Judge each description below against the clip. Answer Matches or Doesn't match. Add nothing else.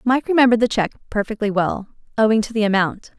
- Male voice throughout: Doesn't match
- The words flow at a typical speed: Matches